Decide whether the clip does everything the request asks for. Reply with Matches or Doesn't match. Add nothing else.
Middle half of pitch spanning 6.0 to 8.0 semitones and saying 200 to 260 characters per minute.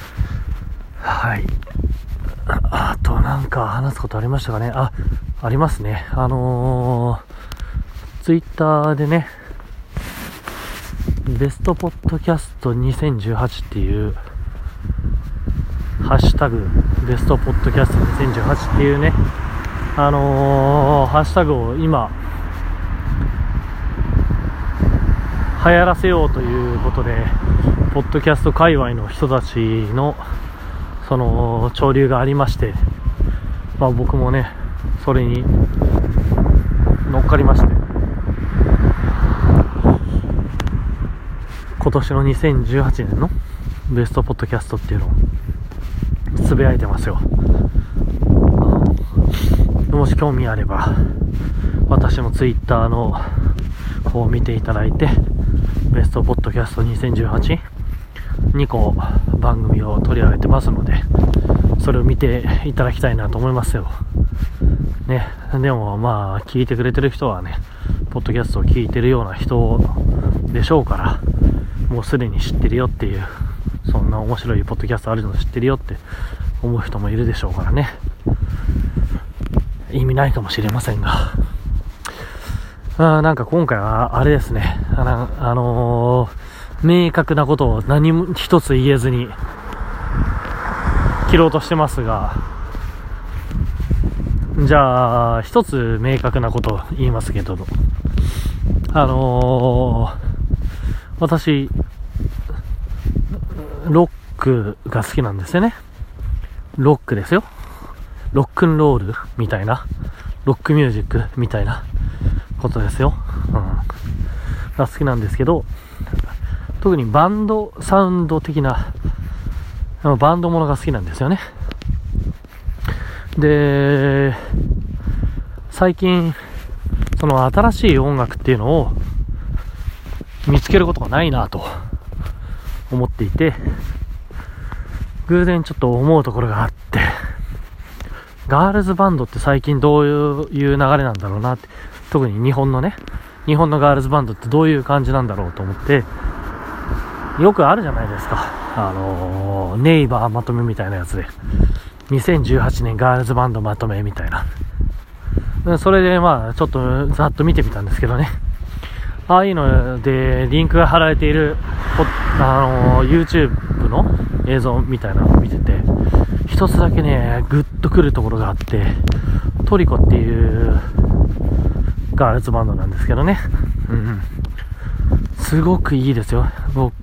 Matches